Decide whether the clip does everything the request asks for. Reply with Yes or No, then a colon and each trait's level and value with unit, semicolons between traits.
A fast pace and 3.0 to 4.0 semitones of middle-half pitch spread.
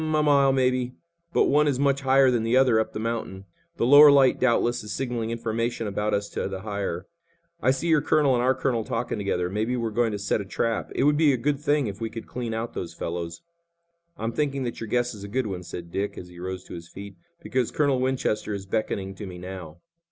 No: fast, 240 wpm; average, 4.7 semitones